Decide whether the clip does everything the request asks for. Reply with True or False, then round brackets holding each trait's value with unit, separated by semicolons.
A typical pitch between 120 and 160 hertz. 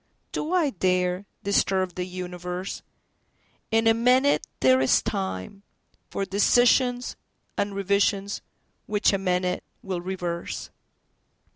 False (195 Hz)